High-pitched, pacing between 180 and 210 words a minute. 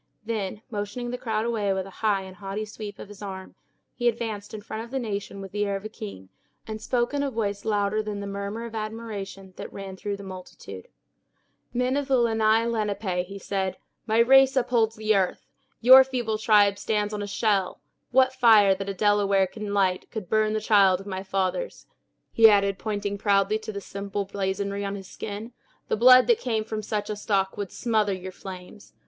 Yes: high, 210 Hz; fast, 205 wpm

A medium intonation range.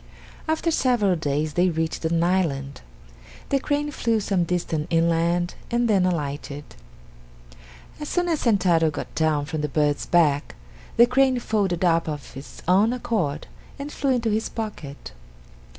No: wide, 6.9 semitones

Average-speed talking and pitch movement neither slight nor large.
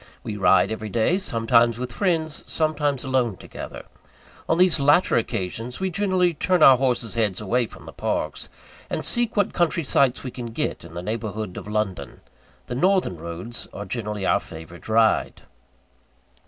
No: average, 165 wpm; wide, 6.8 semitones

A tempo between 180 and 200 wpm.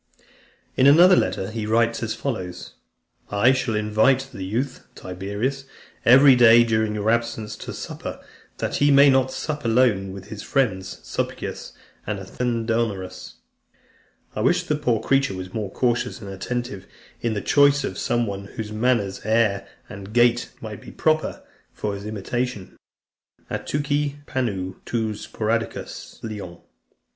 No: average, 145 wpm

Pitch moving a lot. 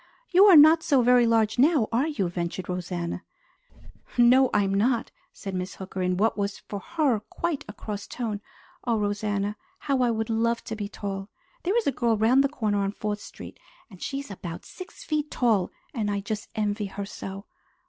No: average, 4.1 semitones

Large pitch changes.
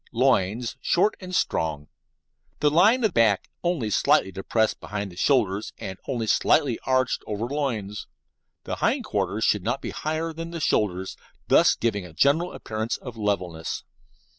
Yes: wide, 6.8 semitones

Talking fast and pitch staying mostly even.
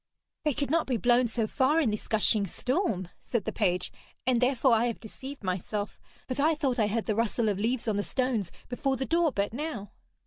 No: fast, 215 wpm; average, 4.1 semitones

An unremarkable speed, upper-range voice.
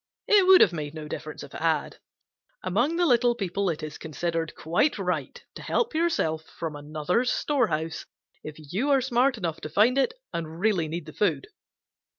No: average, 180 wpm; medium, 175 Hz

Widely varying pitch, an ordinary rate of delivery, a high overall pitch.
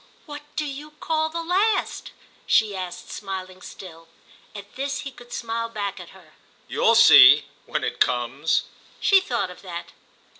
Yes: wide, 8.1 semitones; average, 150 wpm; high, 215 Hz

